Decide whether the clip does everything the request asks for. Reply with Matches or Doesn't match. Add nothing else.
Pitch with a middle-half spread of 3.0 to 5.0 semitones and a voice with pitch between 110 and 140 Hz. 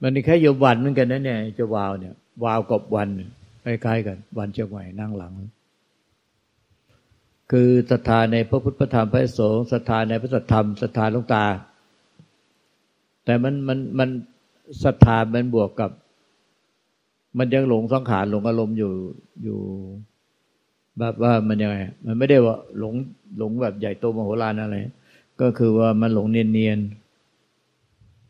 Doesn't match